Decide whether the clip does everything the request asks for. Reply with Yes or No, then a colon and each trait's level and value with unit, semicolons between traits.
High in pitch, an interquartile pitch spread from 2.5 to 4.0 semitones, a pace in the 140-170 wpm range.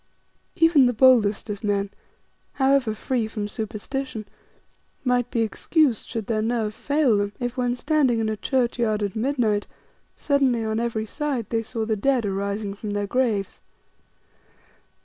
Yes: high, 230 Hz; average, 3.4 semitones; average, 150 wpm